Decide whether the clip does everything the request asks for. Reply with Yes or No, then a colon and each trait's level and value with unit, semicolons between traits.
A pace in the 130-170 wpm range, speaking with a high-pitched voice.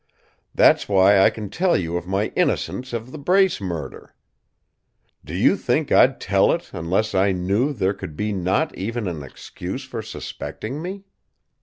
No: average, 165 wpm; low, 100 Hz